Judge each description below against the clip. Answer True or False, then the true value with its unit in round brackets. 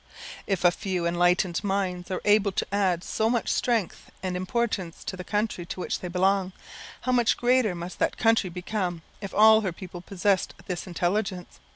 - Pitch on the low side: False (190 Hz)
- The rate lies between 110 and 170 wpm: False (180 wpm)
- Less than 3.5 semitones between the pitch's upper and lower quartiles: True (2.9 semitones)